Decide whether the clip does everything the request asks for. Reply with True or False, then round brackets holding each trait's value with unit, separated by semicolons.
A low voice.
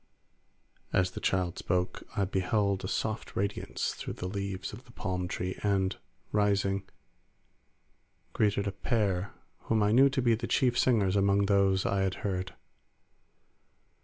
True (100 Hz)